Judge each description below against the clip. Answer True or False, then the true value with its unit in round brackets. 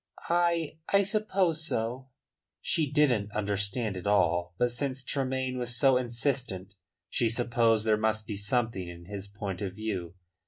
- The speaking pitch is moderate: False (115 Hz)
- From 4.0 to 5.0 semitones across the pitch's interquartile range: True (4.7 semitones)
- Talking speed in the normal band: True (150 wpm)